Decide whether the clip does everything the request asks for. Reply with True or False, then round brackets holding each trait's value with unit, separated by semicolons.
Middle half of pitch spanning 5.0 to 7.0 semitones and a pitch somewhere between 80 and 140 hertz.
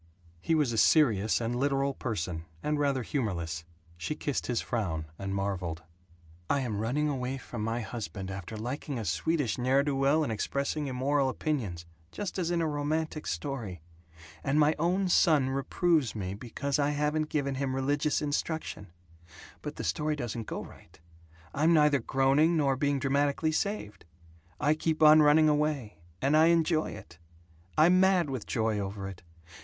True (5.5 semitones; 135 Hz)